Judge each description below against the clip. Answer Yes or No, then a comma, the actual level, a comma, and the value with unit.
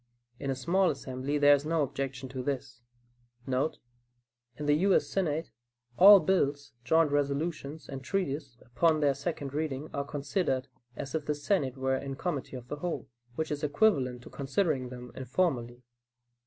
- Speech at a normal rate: Yes, average, 160 wpm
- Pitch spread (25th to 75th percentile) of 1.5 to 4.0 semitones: Yes, average, 3.2 semitones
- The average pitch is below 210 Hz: Yes, medium, 140 Hz